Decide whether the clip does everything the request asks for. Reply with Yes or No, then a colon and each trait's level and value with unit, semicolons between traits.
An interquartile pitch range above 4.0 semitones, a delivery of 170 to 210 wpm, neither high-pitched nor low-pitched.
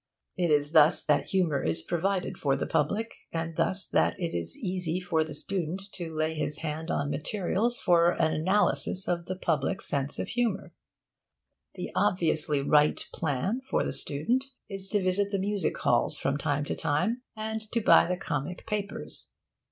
Yes: average, 4.4 semitones; average, 175 wpm; medium, 170 Hz